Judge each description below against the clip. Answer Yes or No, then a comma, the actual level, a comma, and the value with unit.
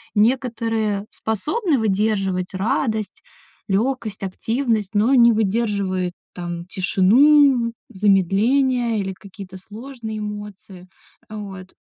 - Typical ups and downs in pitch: Yes, average, 3.5 semitones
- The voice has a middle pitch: No, high, 210 Hz